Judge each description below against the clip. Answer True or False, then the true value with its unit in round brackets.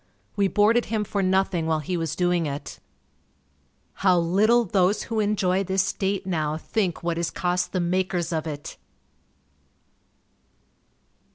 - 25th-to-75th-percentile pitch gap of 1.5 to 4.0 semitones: True (2.8 semitones)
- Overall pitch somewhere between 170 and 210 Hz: True (185 Hz)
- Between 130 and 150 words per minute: True (140 wpm)